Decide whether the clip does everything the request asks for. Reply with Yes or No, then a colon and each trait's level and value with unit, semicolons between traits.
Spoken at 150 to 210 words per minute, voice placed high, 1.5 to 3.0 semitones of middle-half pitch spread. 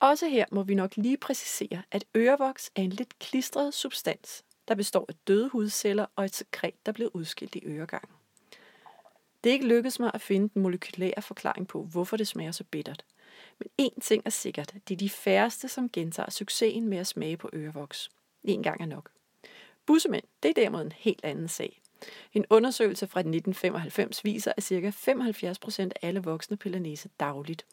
No: average, 185 wpm; high, 205 Hz; average, 3.7 semitones